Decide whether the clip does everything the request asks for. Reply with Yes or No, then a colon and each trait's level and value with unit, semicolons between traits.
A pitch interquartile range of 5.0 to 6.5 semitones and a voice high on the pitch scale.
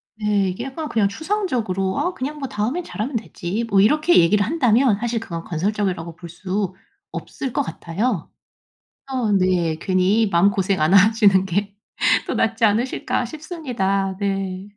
No: average, 4.4 semitones; high, 205 Hz